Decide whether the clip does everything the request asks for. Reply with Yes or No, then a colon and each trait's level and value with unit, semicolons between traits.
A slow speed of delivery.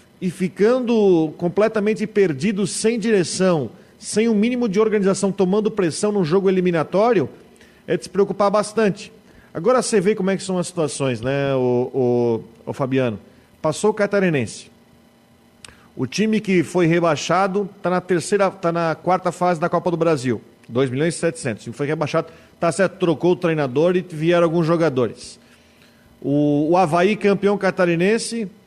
No: average, 160 wpm